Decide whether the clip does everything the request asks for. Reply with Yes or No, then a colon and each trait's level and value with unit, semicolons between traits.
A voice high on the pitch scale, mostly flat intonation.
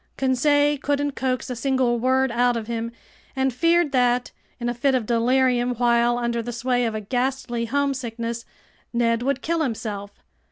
Yes: high, 245 Hz; narrow, 2.1 semitones